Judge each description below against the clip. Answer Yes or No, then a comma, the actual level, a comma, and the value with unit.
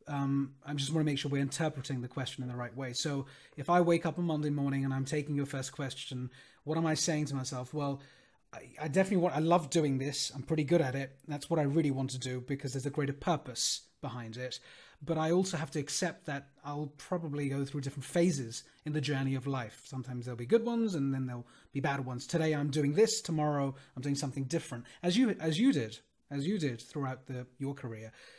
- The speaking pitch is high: No, medium, 140 Hz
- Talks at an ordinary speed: No, fast, 240 wpm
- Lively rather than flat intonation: No, average, 3.0 semitones